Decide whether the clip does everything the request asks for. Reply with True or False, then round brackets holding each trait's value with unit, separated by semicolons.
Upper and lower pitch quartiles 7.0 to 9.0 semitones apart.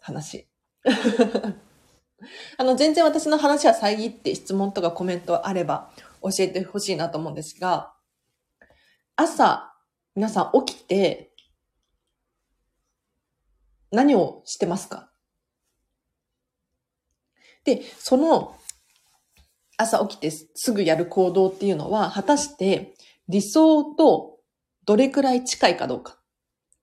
False (6.6 semitones)